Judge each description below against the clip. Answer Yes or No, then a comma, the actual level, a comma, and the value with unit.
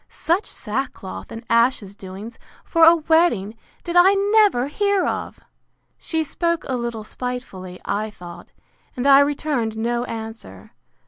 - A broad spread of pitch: Yes, wide, 6.9 semitones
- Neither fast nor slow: No, slow, 130 wpm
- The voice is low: No, high, 245 Hz